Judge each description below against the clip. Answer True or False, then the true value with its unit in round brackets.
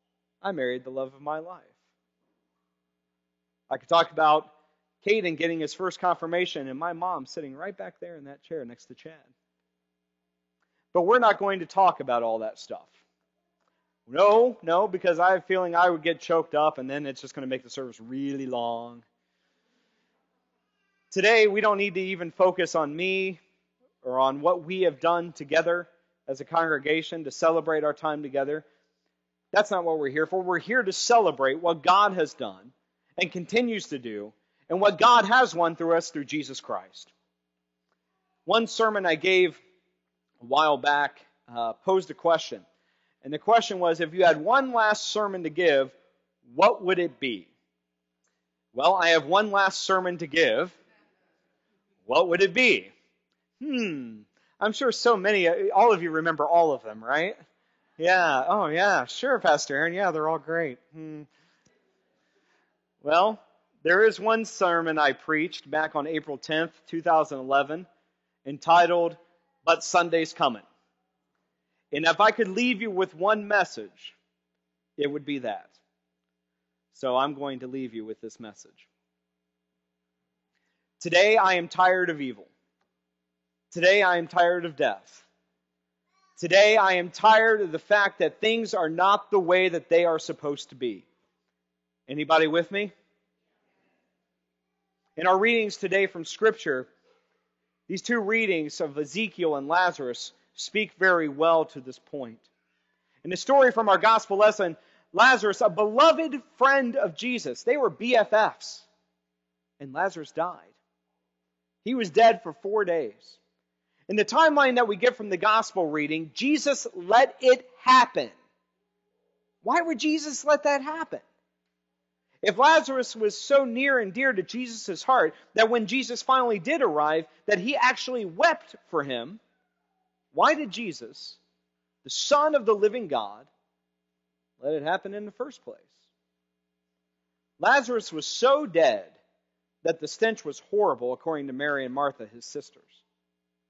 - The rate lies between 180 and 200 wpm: False (155 wpm)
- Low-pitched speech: False (165 Hz)